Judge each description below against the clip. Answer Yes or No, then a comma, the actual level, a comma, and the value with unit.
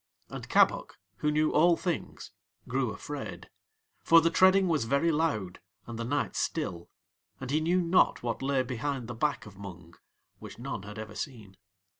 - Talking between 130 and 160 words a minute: No, average, 170 wpm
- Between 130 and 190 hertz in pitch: Yes, medium, 140 Hz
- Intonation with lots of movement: Yes, wide, 6.9 semitones